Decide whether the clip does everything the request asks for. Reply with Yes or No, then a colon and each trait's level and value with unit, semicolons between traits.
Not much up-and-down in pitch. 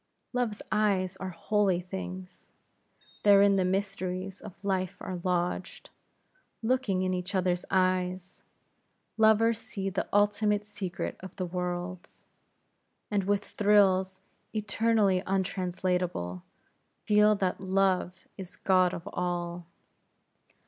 Yes: narrow, 2.0 semitones